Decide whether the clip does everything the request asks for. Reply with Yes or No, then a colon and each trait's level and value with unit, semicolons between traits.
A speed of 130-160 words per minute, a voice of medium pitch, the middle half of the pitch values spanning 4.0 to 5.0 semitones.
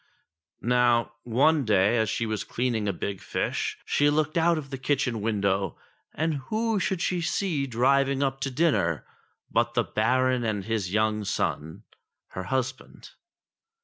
No: average, 150 wpm; low, 125 Hz; average, 4.6 semitones